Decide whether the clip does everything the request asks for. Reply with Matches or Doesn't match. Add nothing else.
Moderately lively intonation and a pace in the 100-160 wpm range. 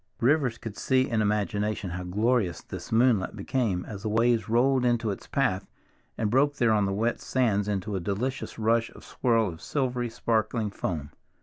Doesn't match